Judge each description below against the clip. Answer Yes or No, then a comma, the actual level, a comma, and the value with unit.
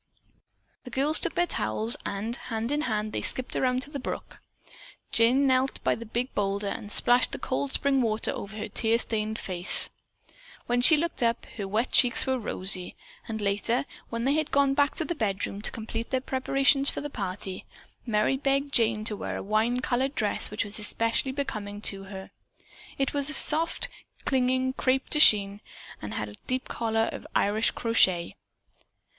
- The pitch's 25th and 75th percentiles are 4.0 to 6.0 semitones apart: Yes, average, 4.3 semitones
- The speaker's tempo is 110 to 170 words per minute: No, average, 185 wpm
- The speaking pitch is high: Yes, high, 230 Hz